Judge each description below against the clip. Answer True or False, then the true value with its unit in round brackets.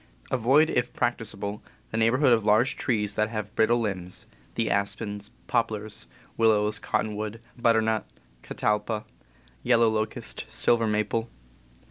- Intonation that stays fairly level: True (1.7 semitones)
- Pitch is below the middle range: True (110 Hz)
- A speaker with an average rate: False (115 wpm)